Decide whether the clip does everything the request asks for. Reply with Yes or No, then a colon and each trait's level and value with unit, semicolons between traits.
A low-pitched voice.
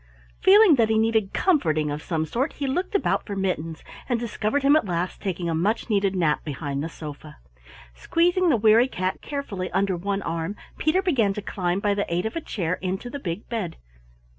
No: high, 200 Hz